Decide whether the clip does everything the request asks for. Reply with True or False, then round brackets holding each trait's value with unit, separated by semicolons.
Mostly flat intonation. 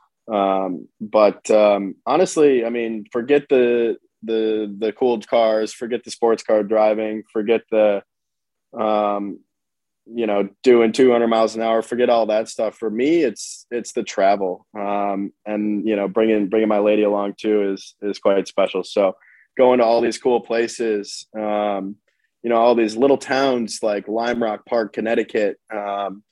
True (2.0 semitones)